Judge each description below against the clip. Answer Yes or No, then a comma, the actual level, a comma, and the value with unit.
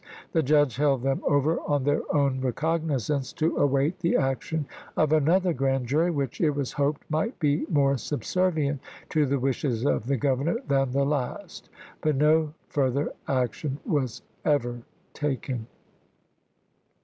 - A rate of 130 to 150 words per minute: Yes, average, 145 wpm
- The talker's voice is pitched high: No, medium, 145 Hz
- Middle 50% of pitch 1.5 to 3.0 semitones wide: Yes, narrow, 2.5 semitones